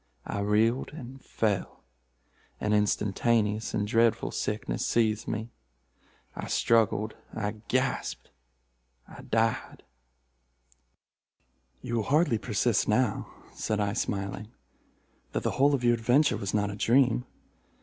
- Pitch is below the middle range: Yes, low, 110 Hz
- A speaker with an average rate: No, slow, 110 wpm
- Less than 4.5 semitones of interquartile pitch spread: Yes, narrow, 2.5 semitones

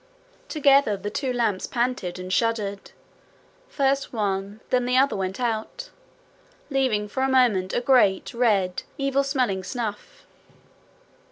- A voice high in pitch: Yes, high, 235 Hz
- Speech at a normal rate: No, slow, 125 wpm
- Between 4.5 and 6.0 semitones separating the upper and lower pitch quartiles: Yes, average, 4.9 semitones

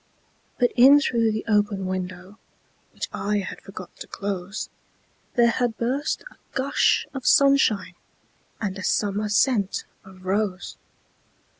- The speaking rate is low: Yes, slow, 115 wpm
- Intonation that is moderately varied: Yes, average, 4.0 semitones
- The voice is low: No, high, 210 Hz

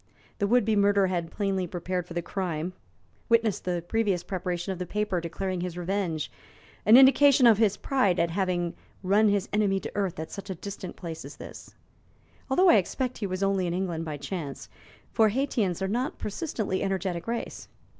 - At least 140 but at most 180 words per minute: No, average, 190 wpm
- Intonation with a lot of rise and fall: No, average, 3.2 semitones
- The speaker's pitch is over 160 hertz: Yes, high, 190 Hz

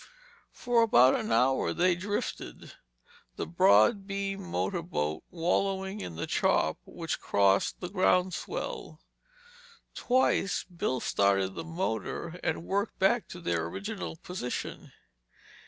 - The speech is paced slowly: Yes, slow, 120 wpm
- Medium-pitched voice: Yes, medium, 180 Hz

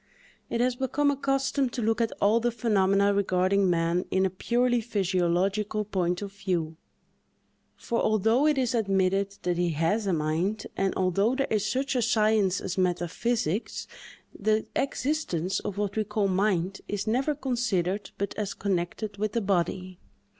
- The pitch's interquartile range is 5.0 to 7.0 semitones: No, average, 3.9 semitones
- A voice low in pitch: No, high, 200 Hz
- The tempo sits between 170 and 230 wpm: No, average, 160 wpm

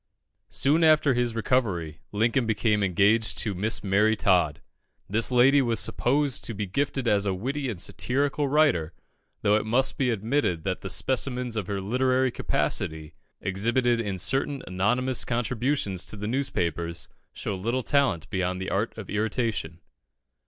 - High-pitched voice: No, low, 110 Hz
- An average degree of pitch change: Yes, average, 5.0 semitones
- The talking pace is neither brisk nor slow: Yes, average, 150 wpm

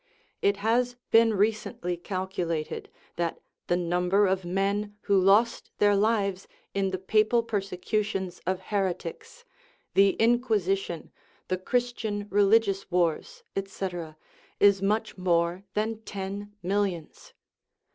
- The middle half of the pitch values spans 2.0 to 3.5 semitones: Yes, narrow, 2.5 semitones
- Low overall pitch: No, high, 195 Hz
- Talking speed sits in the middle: No, slow, 110 wpm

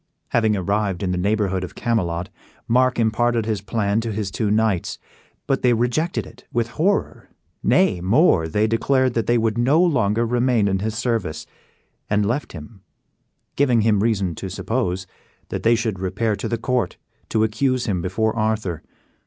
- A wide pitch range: No, average, 3.3 semitones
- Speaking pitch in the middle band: No, low, 110 Hz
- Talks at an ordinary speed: Yes, average, 170 wpm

